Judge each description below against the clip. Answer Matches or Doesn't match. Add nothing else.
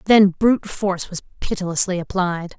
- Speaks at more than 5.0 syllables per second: Matches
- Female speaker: Matches